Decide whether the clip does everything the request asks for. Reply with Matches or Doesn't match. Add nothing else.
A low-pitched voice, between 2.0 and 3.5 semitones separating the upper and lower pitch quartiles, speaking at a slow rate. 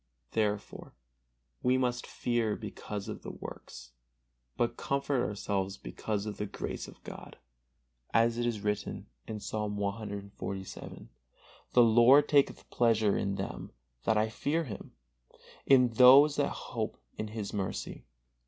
Matches